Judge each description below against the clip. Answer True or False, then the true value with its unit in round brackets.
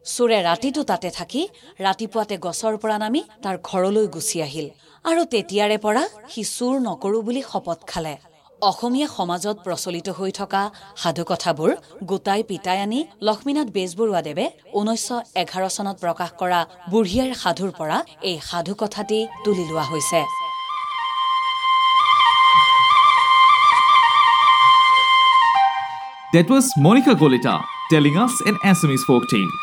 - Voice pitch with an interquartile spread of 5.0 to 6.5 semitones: True (5.6 semitones)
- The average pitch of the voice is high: True (195 Hz)